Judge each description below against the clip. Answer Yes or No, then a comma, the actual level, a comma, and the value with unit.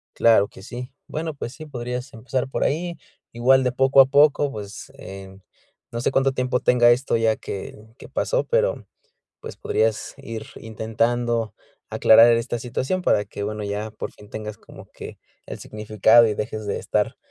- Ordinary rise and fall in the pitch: Yes, average, 3.6 semitones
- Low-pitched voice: Yes, low, 120 Hz